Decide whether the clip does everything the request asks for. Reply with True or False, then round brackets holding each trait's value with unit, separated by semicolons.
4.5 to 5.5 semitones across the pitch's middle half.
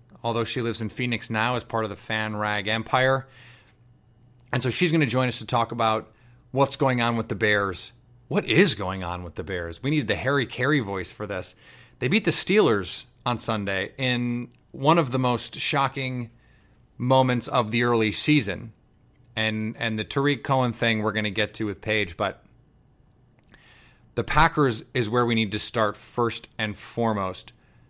False (2.8 semitones)